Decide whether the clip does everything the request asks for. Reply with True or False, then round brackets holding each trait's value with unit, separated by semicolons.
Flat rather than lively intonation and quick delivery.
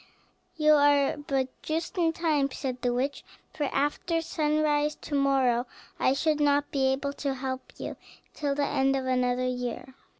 False (2.2 semitones; 165 wpm)